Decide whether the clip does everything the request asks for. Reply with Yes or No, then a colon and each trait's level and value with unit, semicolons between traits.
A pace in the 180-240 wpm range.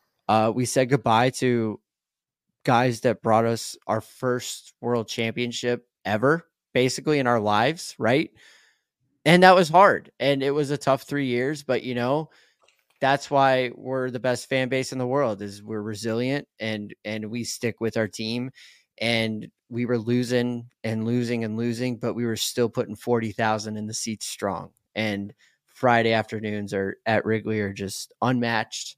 No: average, 165 wpm